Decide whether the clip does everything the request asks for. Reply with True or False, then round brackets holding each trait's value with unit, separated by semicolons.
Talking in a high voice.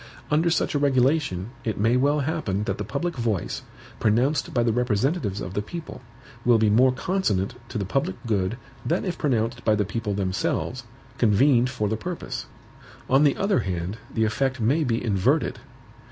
False (120 Hz)